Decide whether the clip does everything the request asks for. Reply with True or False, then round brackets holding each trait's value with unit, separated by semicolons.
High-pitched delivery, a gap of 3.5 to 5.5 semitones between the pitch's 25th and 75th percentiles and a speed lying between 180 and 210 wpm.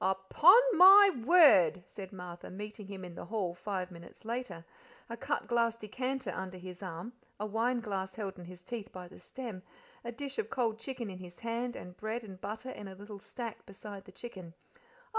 True (210 Hz; 4.4 semitones; 190 wpm)